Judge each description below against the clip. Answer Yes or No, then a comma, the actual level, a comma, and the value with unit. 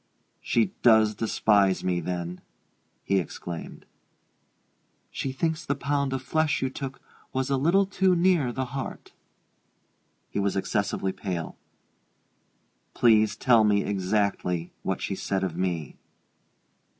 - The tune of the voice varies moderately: No, wide, 6.1 semitones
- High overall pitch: No, low, 110 Hz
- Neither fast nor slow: No, slow, 125 wpm